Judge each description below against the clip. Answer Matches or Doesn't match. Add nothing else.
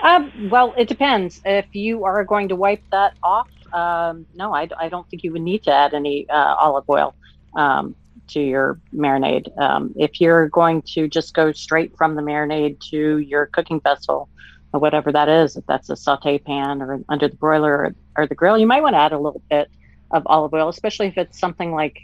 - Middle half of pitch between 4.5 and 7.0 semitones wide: Doesn't match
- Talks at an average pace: Doesn't match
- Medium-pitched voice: Matches